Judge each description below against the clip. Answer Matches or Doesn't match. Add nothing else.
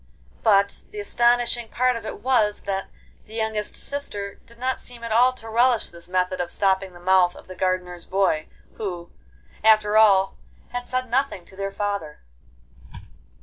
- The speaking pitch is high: Matches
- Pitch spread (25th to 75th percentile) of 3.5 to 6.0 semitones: Matches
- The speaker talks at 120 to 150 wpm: Doesn't match